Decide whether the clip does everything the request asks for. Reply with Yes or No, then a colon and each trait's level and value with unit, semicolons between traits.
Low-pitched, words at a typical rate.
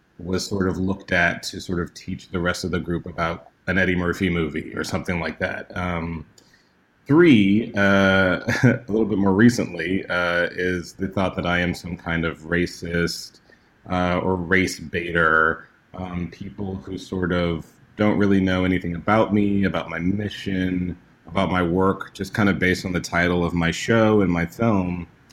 Yes: very low, 90 Hz; average, 180 wpm